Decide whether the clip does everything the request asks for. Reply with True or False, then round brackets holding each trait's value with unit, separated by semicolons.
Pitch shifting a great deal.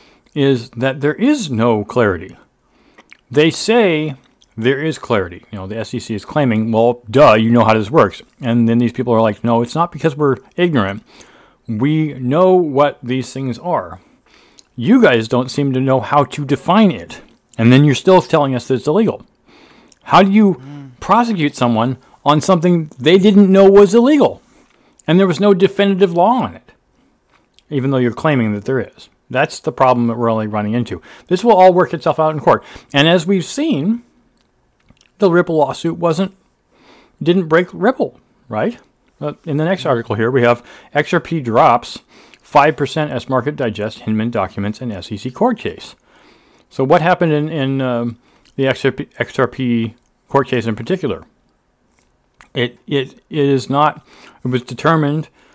True (6.3 semitones)